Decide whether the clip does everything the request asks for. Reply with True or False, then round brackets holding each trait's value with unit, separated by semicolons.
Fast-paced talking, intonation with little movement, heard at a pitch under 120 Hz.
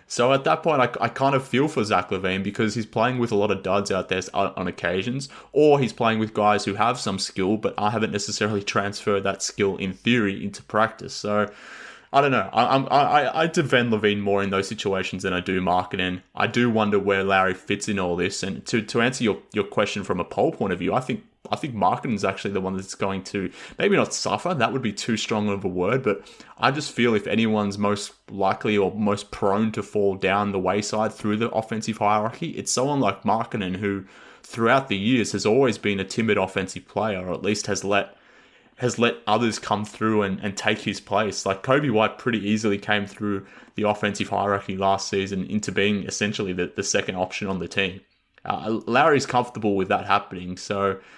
True (215 wpm; 2.2 semitones; 105 Hz)